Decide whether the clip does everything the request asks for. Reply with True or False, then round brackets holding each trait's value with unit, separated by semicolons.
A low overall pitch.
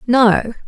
False (235 Hz)